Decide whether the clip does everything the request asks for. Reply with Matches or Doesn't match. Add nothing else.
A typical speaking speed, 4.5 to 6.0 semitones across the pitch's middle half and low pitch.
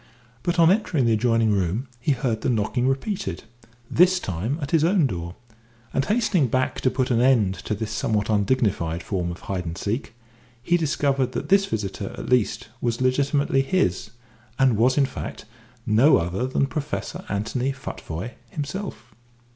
Matches